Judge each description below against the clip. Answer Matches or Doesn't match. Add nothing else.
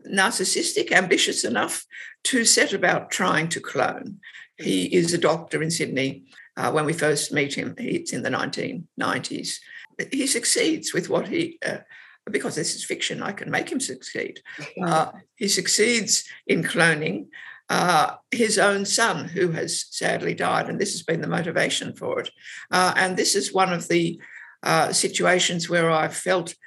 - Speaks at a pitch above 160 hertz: Matches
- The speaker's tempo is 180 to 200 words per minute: Doesn't match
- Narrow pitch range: Doesn't match